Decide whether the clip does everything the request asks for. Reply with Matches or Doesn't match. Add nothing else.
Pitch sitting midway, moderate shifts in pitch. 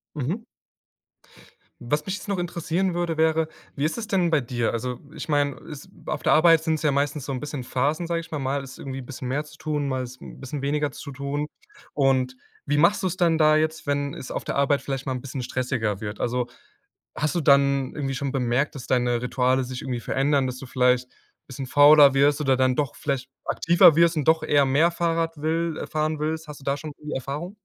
Matches